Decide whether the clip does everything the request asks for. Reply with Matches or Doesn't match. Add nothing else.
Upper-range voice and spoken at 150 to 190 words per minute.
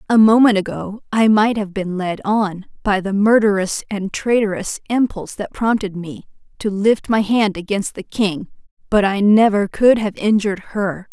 Matches